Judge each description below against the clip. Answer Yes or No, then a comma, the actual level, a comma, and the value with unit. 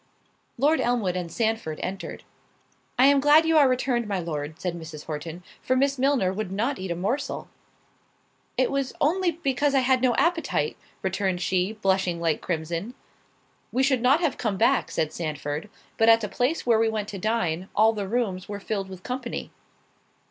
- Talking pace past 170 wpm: Yes, average, 180 wpm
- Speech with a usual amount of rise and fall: No, wide, 6.1 semitones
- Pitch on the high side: Yes, high, 220 Hz